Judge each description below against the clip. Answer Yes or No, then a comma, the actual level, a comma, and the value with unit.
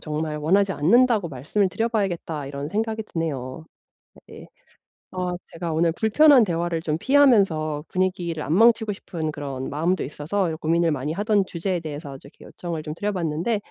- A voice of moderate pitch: Yes, medium, 170 Hz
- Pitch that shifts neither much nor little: Yes, average, 4.9 semitones